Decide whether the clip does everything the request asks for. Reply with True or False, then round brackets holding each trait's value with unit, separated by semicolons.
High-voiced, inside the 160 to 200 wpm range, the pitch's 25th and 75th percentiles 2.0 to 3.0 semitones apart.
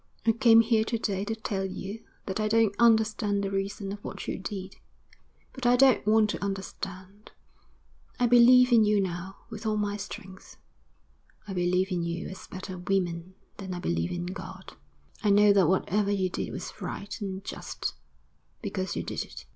True (200 Hz; 180 wpm; 2.5 semitones)